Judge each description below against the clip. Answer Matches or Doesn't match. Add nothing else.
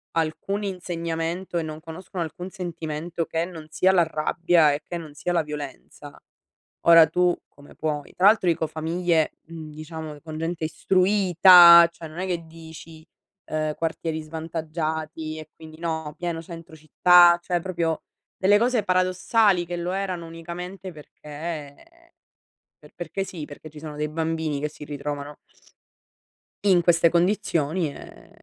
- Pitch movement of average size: Doesn't match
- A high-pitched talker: Doesn't match